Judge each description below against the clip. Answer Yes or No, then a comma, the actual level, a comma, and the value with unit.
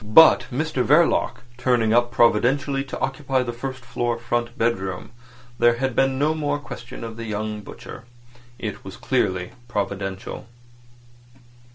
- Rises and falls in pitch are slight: No, average, 3.1 semitones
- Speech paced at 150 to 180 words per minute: No, average, 140 wpm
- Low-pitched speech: Yes, low, 120 Hz